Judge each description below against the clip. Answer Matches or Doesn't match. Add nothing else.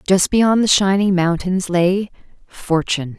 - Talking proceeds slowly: Matches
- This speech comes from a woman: Matches